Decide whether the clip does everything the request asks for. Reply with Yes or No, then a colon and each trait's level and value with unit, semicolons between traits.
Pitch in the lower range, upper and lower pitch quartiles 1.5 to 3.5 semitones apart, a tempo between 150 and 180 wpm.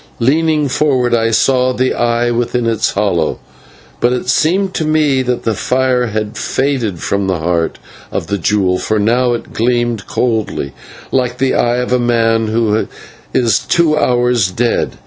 Yes: low, 120 Hz; average, 2.8 semitones; average, 165 wpm